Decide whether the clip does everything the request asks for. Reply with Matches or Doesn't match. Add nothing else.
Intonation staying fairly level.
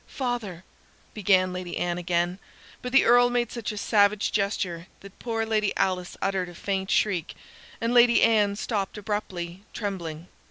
Doesn't match